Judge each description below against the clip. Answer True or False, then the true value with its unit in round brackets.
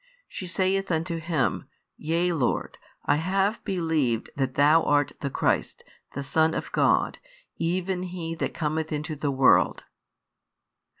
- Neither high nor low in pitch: True (160 Hz)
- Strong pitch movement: False (3.4 semitones)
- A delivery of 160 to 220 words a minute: False (135 wpm)